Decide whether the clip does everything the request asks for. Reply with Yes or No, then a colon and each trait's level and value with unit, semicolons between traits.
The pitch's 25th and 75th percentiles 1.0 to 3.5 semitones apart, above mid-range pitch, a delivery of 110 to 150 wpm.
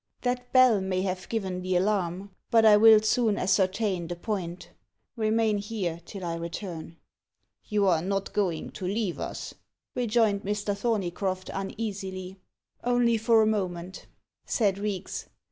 Yes: average, 3.0 semitones; high, 200 Hz; average, 140 wpm